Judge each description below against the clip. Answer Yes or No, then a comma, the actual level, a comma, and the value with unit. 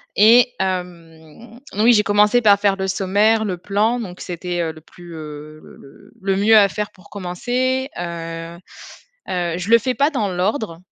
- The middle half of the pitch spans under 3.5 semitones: No, average, 4.1 semitones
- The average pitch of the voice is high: Yes, high, 195 Hz